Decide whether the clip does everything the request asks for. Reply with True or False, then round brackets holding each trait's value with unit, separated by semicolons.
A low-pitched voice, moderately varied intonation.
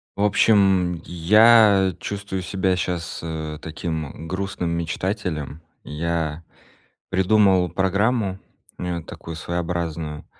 True (90 Hz; 3.0 semitones)